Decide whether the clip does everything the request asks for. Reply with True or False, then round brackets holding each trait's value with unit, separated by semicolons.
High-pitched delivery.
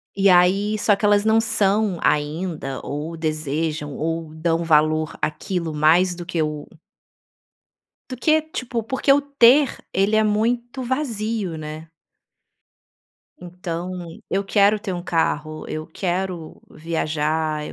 False (175 Hz)